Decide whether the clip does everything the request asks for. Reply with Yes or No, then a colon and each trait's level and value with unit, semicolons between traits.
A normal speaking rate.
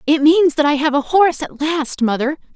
No: fast, 235 wpm